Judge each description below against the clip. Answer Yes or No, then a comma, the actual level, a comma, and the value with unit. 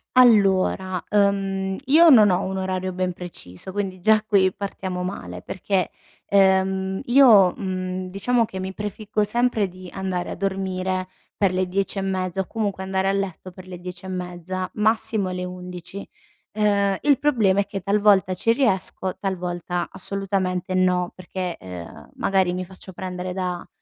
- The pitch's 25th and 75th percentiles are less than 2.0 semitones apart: Yes, narrow, 1.5 semitones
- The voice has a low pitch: No, high, 190 Hz